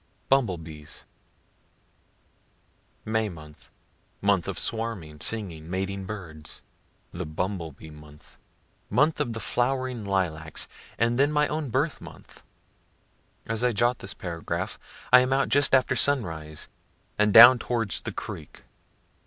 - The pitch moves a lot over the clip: Yes, wide, 7.2 semitones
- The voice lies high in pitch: No, low, 100 Hz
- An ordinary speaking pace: No, slow, 130 wpm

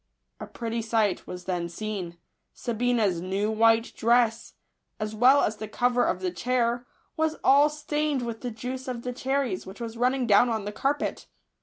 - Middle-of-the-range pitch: No, high, 235 Hz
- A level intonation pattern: No, average, 3.0 semitones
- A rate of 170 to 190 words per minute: Yes, average, 175 wpm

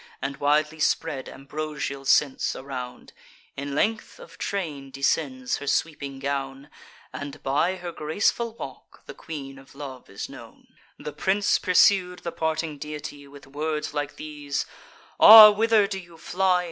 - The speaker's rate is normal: Yes, average, 145 wpm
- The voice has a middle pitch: Yes, medium, 150 Hz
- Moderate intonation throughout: Yes, average, 3.8 semitones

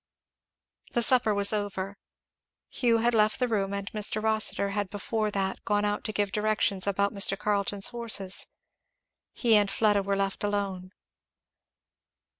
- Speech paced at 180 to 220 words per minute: No, average, 145 wpm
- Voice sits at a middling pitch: No, high, 205 Hz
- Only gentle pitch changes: Yes, narrow, 1.4 semitones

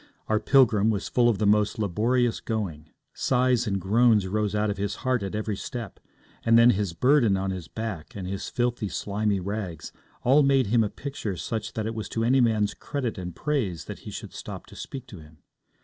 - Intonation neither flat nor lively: Yes, average, 3.5 semitones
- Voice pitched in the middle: No, low, 110 Hz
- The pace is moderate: No, fast, 210 wpm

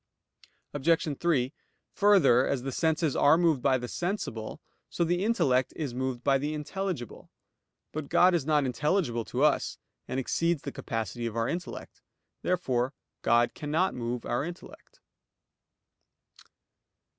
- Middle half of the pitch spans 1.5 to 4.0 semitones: No, average, 5.3 semitones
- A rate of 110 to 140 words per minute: Yes, slow, 135 wpm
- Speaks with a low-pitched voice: No, medium, 145 Hz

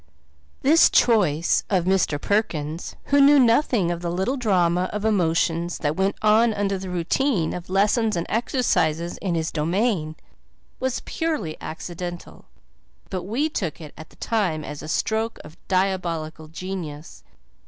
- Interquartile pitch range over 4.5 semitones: Yes, average, 5.0 semitones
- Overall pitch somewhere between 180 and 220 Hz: Yes, medium, 185 Hz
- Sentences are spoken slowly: No, average, 145 wpm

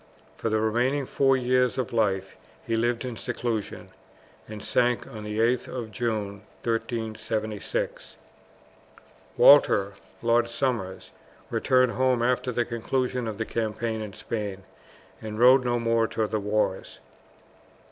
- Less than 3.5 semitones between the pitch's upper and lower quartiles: Yes, narrow, 2.4 semitones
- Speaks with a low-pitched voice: Yes, low, 115 Hz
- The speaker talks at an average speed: No, slow, 130 wpm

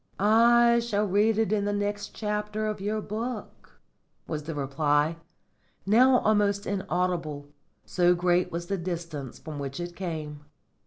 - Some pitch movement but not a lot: Yes, average, 4.3 semitones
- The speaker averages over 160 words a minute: No, average, 145 wpm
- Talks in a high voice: Yes, high, 195 Hz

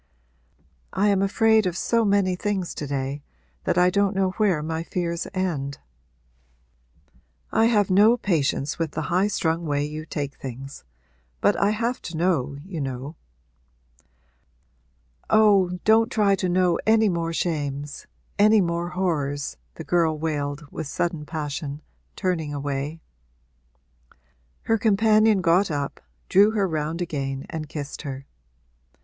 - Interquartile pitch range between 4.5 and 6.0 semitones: Yes, average, 5.2 semitones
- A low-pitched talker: No, medium, 170 Hz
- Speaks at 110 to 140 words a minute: Yes, slow, 135 wpm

